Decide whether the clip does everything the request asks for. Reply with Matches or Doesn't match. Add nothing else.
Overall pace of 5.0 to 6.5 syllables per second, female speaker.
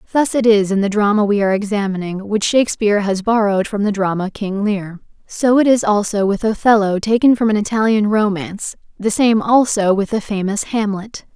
Matches